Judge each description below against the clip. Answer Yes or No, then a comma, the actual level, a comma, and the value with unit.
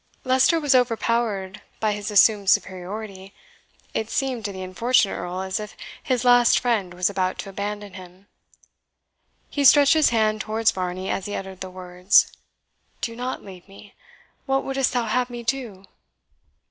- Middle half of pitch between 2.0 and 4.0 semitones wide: No, average, 4.4 semitones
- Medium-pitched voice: No, high, 210 Hz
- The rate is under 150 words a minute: No, average, 160 wpm